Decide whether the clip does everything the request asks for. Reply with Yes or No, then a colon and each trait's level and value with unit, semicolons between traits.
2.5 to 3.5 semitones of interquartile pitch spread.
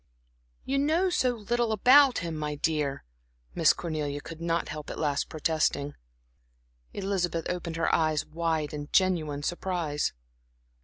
No: average, 4.2 semitones